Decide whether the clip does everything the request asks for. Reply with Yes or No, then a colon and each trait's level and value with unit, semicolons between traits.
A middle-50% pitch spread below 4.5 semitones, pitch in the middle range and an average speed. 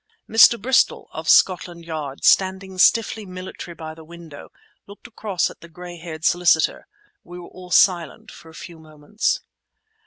Yes: average, 2.8 semitones; medium, 175 Hz; average, 155 wpm